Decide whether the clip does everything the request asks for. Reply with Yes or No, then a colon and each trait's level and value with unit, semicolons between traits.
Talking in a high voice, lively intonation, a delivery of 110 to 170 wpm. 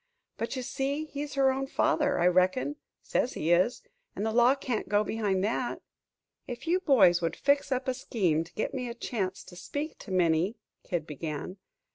No: high, 235 Hz; wide, 6.8 semitones; average, 195 wpm